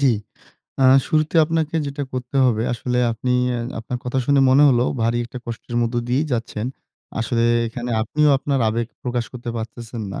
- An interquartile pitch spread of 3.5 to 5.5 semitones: No, average, 2.8 semitones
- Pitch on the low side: Yes, low, 125 Hz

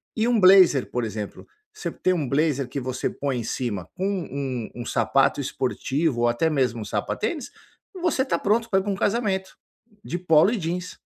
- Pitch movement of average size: No, wide, 7.6 semitones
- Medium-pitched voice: Yes, medium, 160 Hz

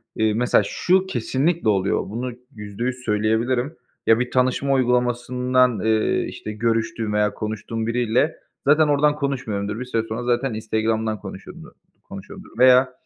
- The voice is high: No, low, 120 Hz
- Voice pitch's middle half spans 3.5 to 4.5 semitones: No, average, 2.8 semitones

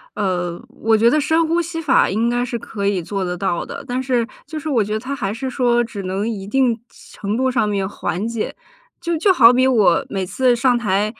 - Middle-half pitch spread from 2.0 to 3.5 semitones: No, average, 4.6 semitones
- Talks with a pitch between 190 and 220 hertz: No, high, 230 Hz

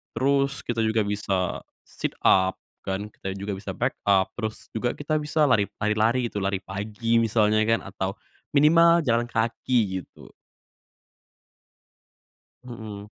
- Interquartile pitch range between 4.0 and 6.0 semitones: No, average, 3.5 semitones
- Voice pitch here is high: No, low, 110 Hz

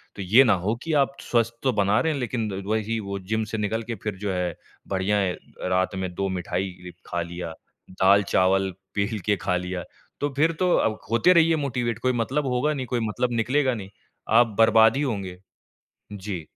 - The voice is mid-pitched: No, low, 105 Hz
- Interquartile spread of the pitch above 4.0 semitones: Yes, average, 4.5 semitones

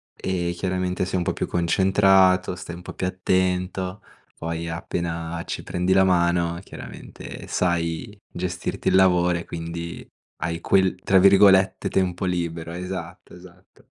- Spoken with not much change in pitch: Yes, narrow, 1.6 semitones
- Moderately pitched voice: No, very low, 90 Hz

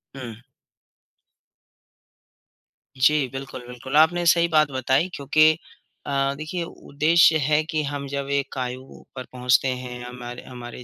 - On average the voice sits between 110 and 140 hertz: Yes, low, 135 Hz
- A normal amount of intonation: Yes, average, 3.5 semitones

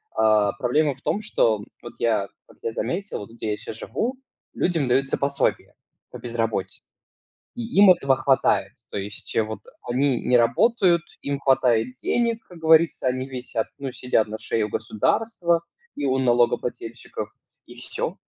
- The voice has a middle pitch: No, low, 130 Hz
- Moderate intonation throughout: No, wide, 5.9 semitones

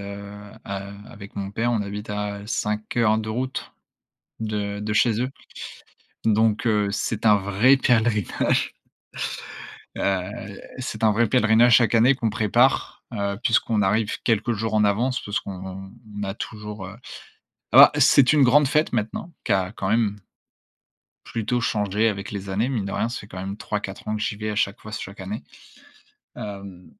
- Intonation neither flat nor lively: No, narrow, 2.2 semitones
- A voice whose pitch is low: Yes, low, 105 Hz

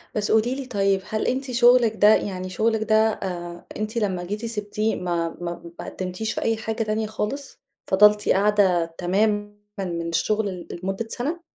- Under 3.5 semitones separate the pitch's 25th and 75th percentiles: Yes, average, 3.0 semitones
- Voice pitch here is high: Yes, high, 210 Hz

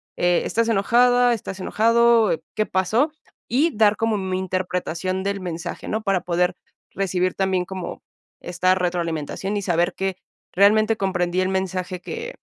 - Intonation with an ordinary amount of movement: Yes, average, 3.1 semitones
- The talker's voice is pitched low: No, high, 190 Hz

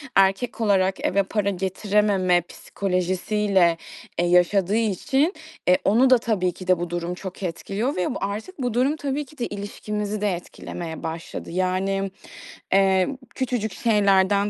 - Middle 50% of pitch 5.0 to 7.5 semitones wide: No, average, 2.9 semitones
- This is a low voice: No, high, 195 Hz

